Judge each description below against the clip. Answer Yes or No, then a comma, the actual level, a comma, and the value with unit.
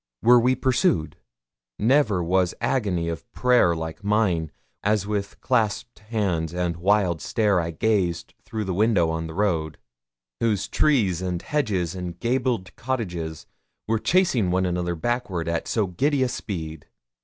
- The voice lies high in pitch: No, very low, 95 Hz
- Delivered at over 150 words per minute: No, average, 145 wpm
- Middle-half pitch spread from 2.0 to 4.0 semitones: No, average, 5.0 semitones